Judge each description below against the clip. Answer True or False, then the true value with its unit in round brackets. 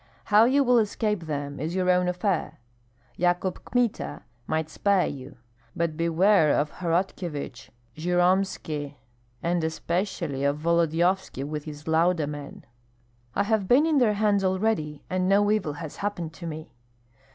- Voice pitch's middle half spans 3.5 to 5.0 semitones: True (4.3 semitones)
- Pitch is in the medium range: True (175 Hz)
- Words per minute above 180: False (140 wpm)